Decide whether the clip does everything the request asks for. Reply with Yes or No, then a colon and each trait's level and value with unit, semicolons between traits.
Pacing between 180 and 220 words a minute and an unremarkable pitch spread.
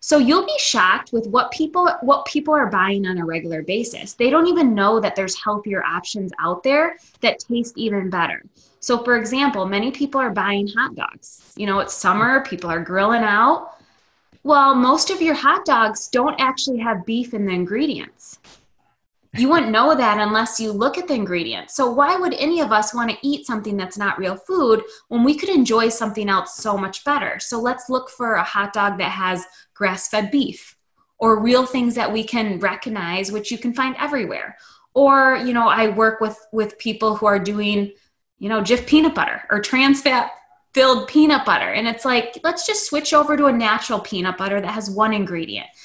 Yes: average, 200 wpm; average, 5.0 semitones